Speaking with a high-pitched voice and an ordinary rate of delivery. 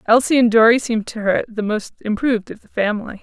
No: high, 225 Hz; fast, 225 wpm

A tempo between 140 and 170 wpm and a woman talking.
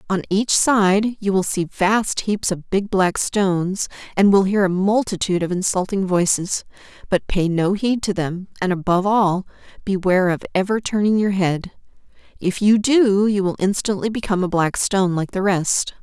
No: average, 180 wpm; female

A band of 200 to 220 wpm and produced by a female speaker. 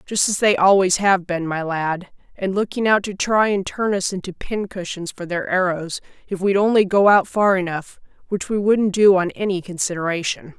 Yes: fast, 205 wpm; female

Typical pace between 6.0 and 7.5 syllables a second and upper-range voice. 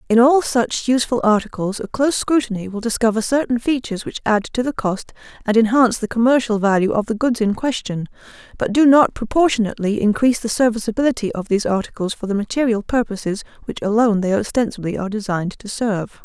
Yes: 6.4 syllables/s; high, 225 Hz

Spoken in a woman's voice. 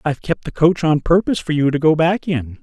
No: male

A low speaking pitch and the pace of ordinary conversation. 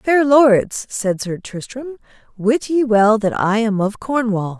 No: high, 225 Hz; average, 170 wpm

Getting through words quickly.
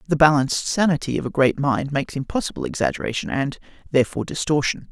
No: average, 160 wpm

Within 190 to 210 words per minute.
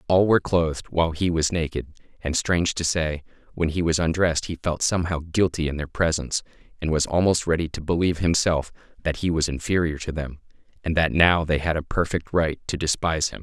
Yes: fast, 205 wpm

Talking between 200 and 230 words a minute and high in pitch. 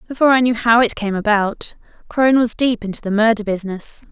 Yes: fast, 205 wpm; high, 225 Hz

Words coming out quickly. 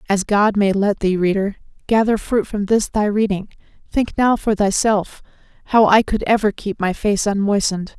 No: average, 180 wpm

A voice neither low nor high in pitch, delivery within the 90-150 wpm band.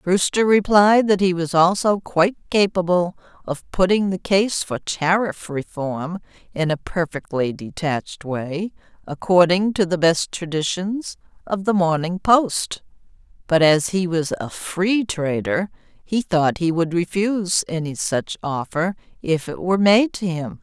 Yes: medium, 180 Hz; average, 145 wpm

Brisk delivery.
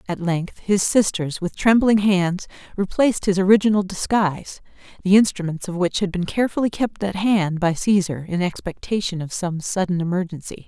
No: average, 165 wpm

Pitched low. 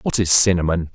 Yes: very low, 85 Hz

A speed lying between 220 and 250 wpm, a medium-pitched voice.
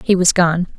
Yes: fast, 230 wpm; medium, 175 Hz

